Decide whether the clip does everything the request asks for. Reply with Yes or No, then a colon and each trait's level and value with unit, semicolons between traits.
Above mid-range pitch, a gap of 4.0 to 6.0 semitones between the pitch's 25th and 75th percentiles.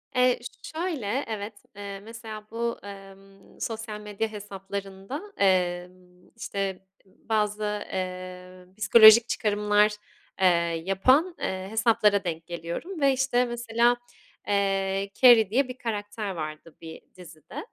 No: high, 205 Hz; average, 3.2 semitones